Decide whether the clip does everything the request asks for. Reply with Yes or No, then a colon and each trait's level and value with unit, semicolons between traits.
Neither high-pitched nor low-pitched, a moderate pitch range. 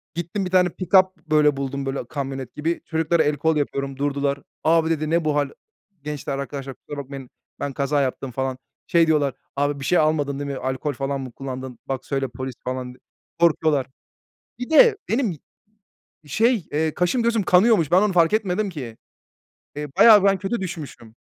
Yes: medium, 150 Hz; average, 4.2 semitones